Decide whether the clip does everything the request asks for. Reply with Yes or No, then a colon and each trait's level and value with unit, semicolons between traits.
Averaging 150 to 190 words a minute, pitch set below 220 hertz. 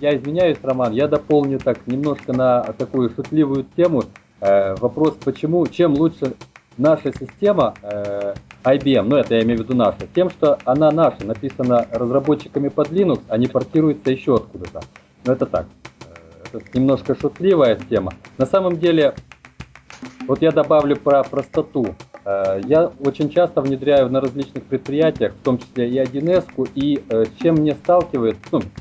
Yes: fast, 160 wpm; medium, 140 Hz